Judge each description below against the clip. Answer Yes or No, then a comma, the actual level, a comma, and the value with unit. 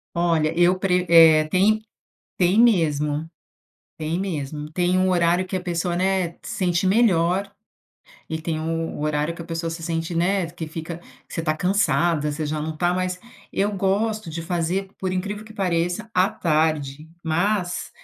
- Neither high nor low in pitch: Yes, medium, 175 Hz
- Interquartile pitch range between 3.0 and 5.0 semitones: No, narrow, 2.6 semitones